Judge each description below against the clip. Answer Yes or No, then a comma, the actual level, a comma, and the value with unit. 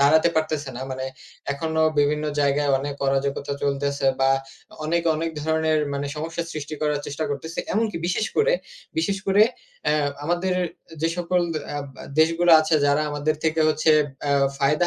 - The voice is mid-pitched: Yes, medium, 155 Hz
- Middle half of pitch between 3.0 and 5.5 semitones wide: No, narrow, 2.6 semitones